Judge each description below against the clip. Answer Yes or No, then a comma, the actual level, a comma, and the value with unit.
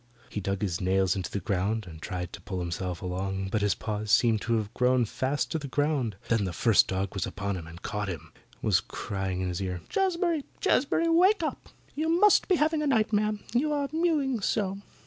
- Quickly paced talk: Yes, fast, 210 wpm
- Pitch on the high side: No, low, 110 Hz